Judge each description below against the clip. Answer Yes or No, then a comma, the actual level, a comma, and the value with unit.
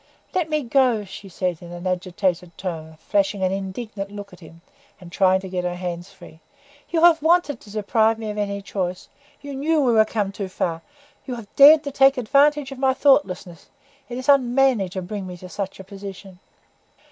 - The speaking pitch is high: Yes, high, 200 Hz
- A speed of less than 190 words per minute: No, average, 200 wpm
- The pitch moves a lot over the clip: Yes, wide, 6.2 semitones